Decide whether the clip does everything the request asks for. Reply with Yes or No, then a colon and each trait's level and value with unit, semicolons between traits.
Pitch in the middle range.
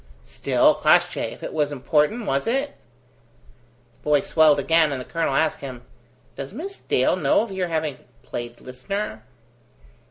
Yes: medium, 150 Hz